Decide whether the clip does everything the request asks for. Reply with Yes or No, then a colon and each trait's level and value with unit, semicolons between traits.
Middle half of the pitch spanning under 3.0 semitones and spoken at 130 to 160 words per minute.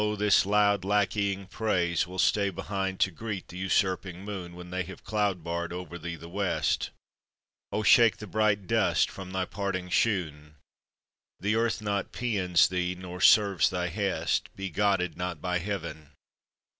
Yes: narrow, 2.4 semitones; average, 155 wpm